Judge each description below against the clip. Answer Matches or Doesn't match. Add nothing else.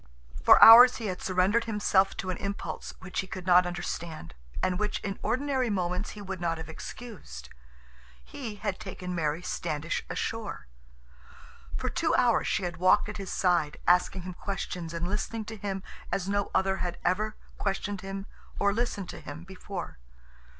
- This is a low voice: Doesn't match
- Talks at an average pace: Matches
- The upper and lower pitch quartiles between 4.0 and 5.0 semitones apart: Doesn't match